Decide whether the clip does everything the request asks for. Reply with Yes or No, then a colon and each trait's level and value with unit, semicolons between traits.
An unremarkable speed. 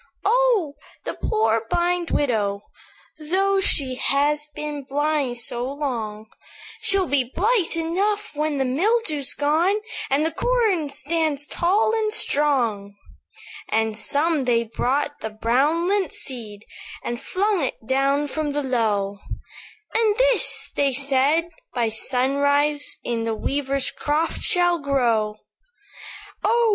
No: slow, 125 wpm